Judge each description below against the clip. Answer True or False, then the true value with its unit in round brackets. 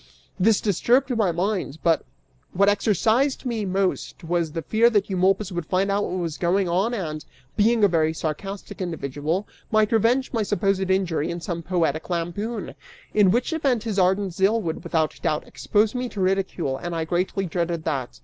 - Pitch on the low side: False (190 Hz)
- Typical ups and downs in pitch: True (3.8 semitones)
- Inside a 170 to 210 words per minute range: True (180 wpm)